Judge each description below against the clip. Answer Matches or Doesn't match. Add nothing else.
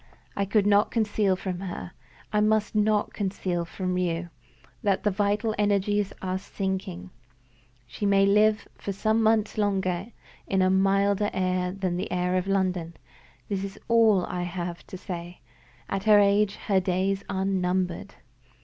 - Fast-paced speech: Doesn't match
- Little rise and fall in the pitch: Matches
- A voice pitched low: Doesn't match